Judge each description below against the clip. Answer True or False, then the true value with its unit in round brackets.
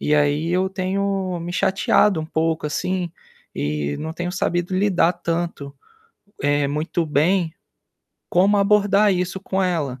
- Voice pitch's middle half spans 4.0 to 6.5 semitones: False (3.5 semitones)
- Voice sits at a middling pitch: True (175 Hz)